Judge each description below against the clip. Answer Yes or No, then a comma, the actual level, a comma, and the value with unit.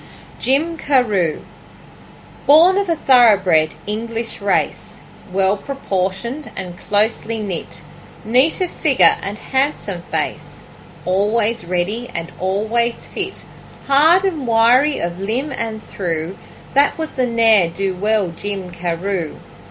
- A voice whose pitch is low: No, high, 215 Hz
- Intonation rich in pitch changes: Yes, wide, 5.8 semitones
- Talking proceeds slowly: Yes, slow, 120 wpm